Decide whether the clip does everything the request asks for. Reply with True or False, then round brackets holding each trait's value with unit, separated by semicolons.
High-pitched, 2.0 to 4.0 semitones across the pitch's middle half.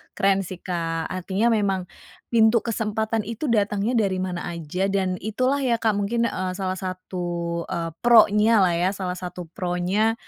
True (195 Hz; 3.4 semitones)